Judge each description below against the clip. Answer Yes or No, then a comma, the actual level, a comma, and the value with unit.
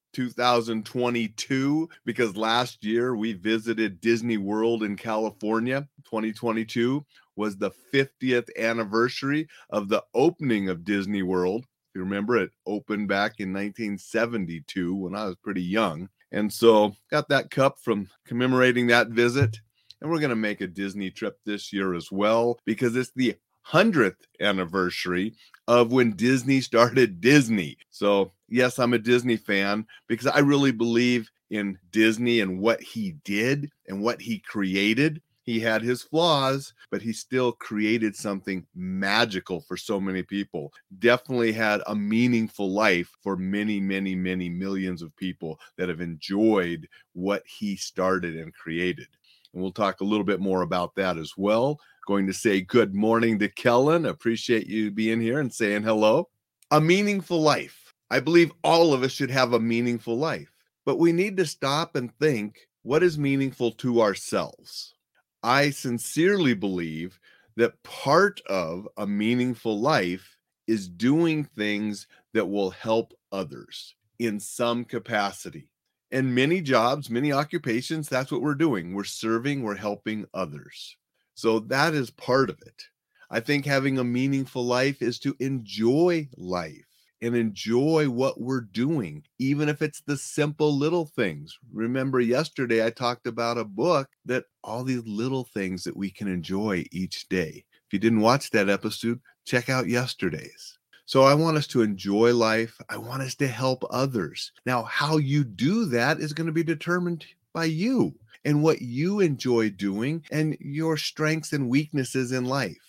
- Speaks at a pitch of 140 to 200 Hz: No, low, 115 Hz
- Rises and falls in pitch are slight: No, average, 4.8 semitones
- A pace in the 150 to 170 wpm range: Yes, average, 155 wpm